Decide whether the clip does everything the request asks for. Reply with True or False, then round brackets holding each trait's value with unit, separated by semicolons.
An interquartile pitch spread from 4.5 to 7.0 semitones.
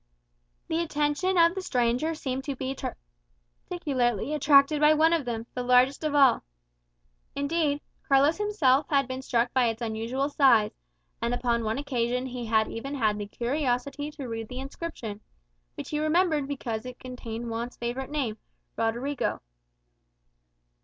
False (3.8 semitones)